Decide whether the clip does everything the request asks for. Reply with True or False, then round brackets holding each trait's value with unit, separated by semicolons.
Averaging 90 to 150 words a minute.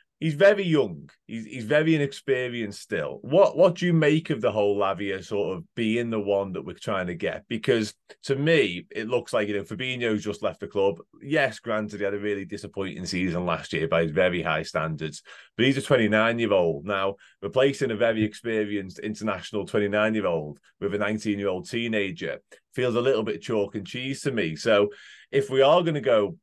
False (195 wpm)